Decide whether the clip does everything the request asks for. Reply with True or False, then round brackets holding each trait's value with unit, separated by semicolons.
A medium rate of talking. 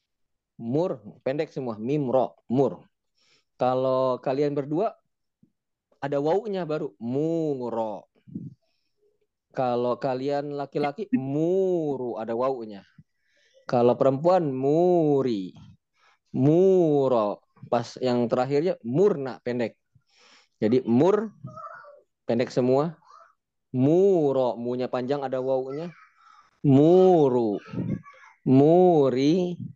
False (80 wpm)